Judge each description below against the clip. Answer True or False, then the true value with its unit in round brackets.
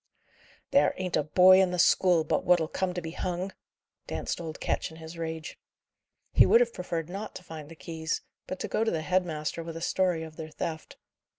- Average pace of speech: False (215 wpm)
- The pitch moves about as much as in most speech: False (2.3 semitones)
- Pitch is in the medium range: True (170 Hz)